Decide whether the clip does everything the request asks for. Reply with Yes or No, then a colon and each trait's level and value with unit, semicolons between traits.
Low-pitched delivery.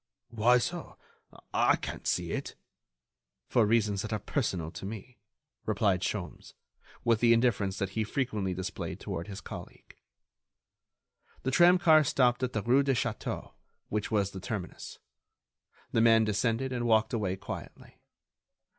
Yes: low, 110 Hz